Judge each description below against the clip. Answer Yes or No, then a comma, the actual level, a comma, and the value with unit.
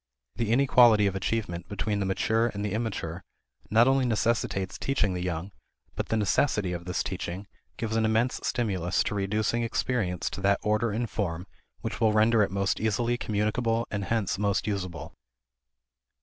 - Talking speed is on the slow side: No, average, 165 wpm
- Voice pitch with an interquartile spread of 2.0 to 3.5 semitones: Yes, average, 3.0 semitones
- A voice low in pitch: Yes, low, 105 Hz